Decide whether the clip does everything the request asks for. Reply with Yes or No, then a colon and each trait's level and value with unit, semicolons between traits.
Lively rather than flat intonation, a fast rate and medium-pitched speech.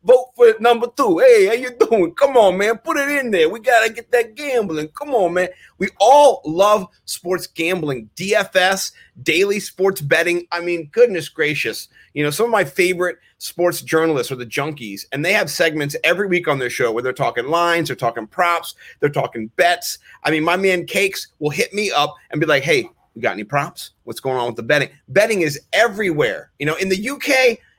Yes: wide, 7.1 semitones; fast, 210 wpm; medium, 180 Hz